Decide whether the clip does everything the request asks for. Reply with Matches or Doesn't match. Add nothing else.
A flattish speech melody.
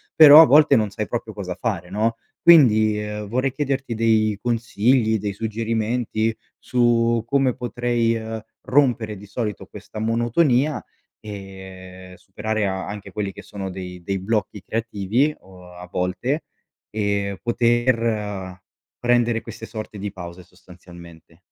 Doesn't match